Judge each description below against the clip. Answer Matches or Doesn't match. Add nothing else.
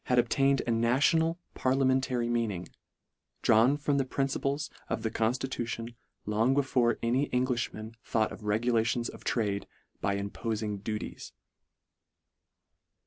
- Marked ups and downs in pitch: Doesn't match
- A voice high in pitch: Doesn't match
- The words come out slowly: Matches